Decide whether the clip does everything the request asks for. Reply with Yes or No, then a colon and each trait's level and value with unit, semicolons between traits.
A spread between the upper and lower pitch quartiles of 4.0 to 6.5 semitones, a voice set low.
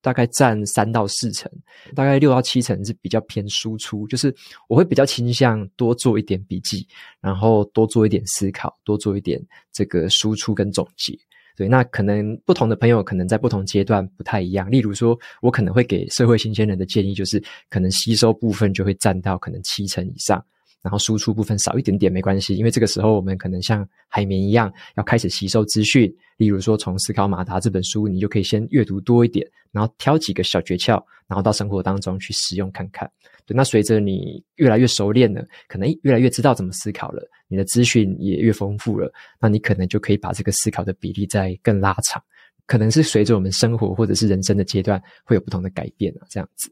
No: average, 3.0 semitones; low, 105 Hz